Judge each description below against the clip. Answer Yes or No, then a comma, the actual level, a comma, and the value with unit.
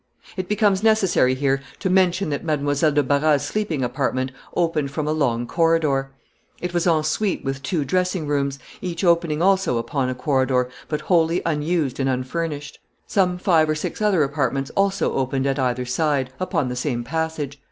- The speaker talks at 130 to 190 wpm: Yes, average, 175 wpm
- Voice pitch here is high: No, medium, 150 Hz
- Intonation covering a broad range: No, average, 4.2 semitones